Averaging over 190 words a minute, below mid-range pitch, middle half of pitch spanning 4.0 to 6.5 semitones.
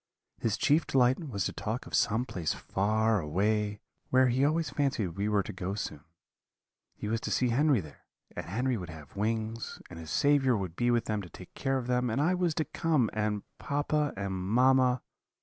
Yes: average, 200 wpm; low, 115 Hz; average, 4.8 semitones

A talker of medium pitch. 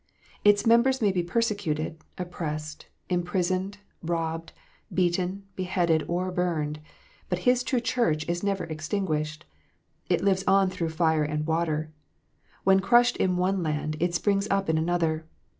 Yes: medium, 175 Hz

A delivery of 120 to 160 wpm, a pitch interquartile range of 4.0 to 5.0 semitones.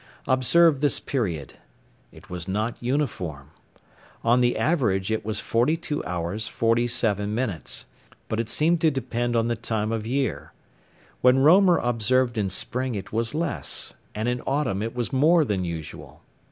Yes: average, 155 wpm; average, 4.3 semitones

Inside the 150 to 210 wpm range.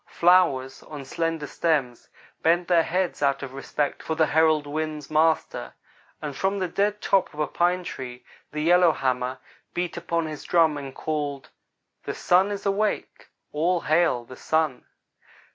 Yes: average, 155 wpm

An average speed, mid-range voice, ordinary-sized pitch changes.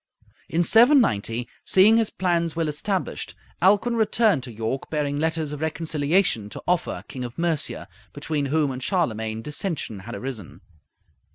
No: average, 145 wpm; medium, 155 Hz; wide, 6.5 semitones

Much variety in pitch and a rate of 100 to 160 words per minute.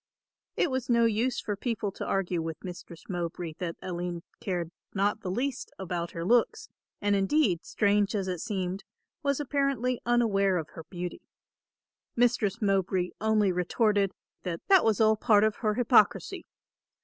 No: average, 4.4 semitones; average, 155 wpm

